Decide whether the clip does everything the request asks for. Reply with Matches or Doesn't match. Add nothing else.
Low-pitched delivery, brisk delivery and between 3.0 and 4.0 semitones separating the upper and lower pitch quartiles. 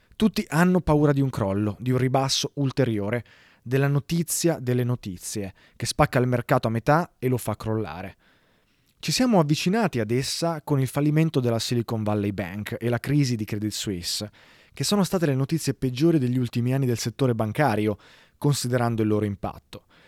Doesn't match